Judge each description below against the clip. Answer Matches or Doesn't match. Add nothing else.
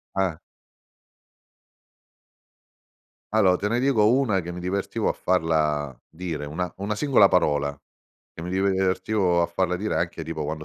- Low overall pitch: Matches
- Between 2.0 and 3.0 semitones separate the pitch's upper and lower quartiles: Doesn't match